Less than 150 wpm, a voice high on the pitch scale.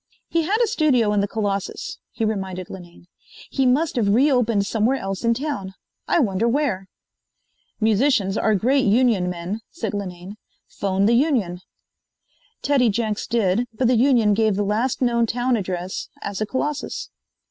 No: average, 160 wpm; high, 220 Hz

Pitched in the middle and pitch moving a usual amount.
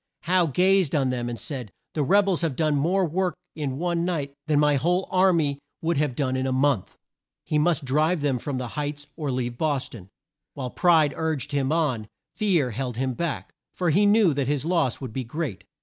Yes: medium, 150 Hz; average, 4.4 semitones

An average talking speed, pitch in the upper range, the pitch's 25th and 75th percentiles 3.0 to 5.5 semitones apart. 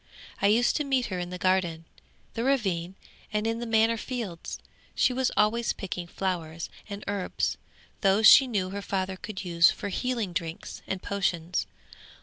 Yes: average, 165 wpm; high, 195 Hz; average, 4.0 semitones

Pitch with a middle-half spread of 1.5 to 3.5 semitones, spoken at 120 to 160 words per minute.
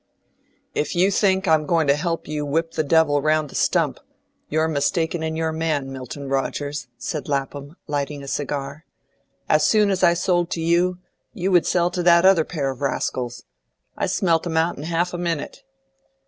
No: average, 3.2 semitones; average, 185 wpm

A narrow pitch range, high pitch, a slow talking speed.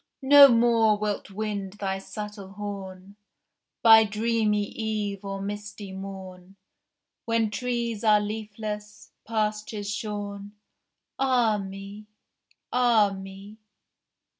Yes: narrow, 1.8 semitones; high, 210 Hz; slow, 95 wpm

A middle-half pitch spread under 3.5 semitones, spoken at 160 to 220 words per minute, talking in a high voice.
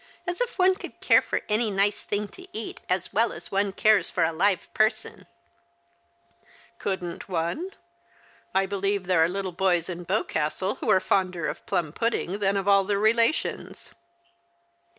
Yes: average, 3.0 semitones; average, 170 wpm; high, 195 Hz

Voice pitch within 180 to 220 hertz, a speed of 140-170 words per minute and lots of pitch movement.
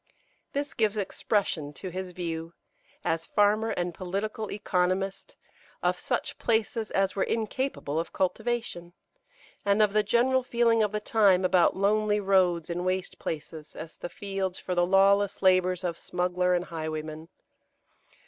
No: high, 190 Hz; average, 145 wpm; average, 3.2 semitones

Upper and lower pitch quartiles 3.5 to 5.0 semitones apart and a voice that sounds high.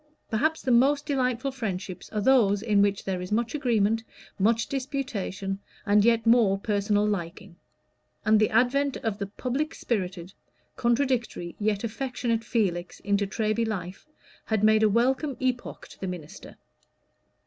Yes: average, 3.8 semitones; high, 220 Hz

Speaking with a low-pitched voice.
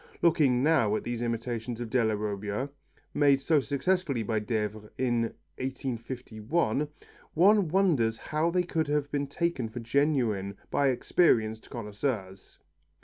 Yes: low, 125 Hz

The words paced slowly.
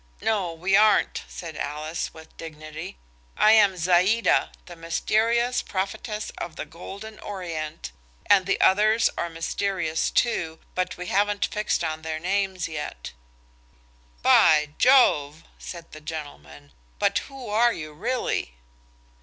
Yes: slow, 130 wpm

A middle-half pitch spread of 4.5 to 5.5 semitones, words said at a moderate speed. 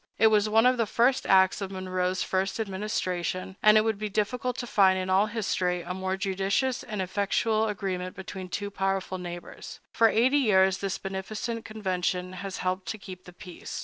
No: narrow, 2.6 semitones; average, 185 wpm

